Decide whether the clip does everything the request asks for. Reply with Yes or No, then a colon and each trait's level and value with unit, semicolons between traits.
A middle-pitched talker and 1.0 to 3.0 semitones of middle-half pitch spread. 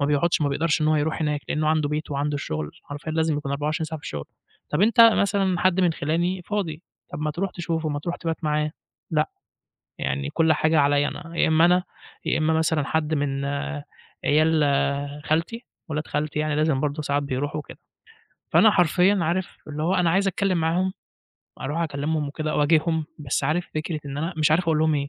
Yes: medium, 155 Hz; narrow, 2.4 semitones